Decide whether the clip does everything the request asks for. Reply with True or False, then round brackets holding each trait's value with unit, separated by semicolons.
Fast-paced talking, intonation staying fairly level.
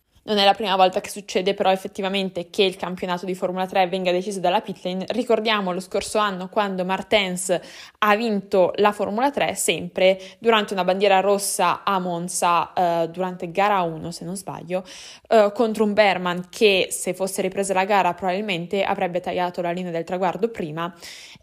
True (175 wpm; 2.2 semitones)